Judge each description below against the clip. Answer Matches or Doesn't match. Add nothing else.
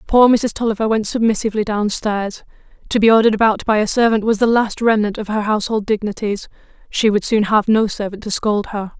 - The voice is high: Matches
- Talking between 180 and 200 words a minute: Matches